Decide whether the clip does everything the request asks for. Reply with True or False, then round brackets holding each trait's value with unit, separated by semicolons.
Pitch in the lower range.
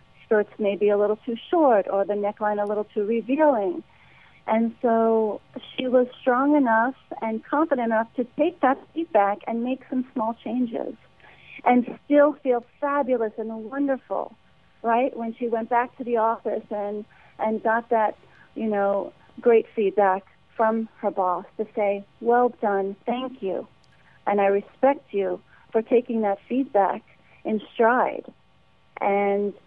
False (225 Hz)